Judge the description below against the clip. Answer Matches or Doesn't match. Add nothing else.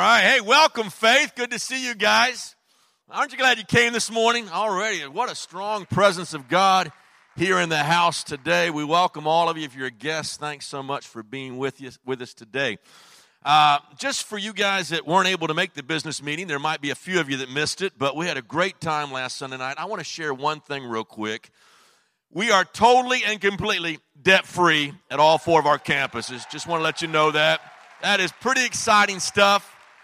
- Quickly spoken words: Matches